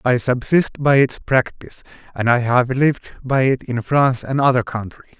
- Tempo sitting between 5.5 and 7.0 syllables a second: No, 5.0 syllables/s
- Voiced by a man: Yes, male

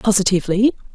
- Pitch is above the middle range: Yes, high, 205 Hz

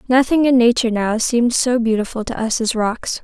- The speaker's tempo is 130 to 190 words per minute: No, fast, 205 wpm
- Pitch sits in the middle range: No, high, 235 Hz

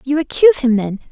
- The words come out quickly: Yes, fast, 215 wpm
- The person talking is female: Yes, female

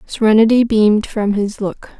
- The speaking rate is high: No, average, 150 wpm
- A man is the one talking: No, female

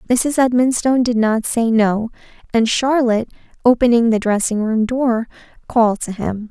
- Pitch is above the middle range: Yes, high, 235 Hz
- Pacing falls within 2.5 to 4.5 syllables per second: No, 4.9 syllables/s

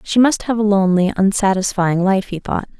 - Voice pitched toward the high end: Yes, high, 195 Hz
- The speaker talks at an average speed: Yes, average, 195 wpm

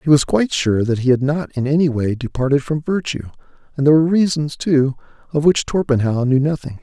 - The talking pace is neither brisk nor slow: No, fast, 210 wpm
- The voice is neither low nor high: Yes, medium, 145 Hz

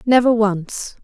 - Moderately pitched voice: No, high, 220 Hz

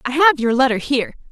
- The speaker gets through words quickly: Yes, fast, 230 wpm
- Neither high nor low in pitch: No, very high, 265 Hz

